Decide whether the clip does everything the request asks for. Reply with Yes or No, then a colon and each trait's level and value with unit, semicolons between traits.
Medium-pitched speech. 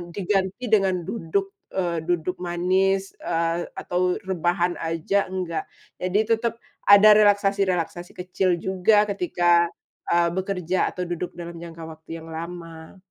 Yes: medium, 180 Hz